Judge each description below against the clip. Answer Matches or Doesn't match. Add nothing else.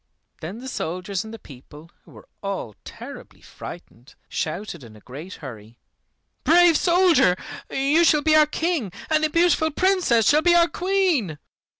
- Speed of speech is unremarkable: Matches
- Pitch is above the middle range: Matches